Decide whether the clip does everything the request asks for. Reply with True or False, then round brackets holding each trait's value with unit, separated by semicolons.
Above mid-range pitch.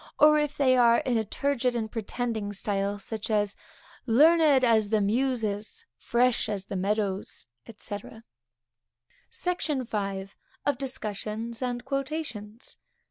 True (230 Hz)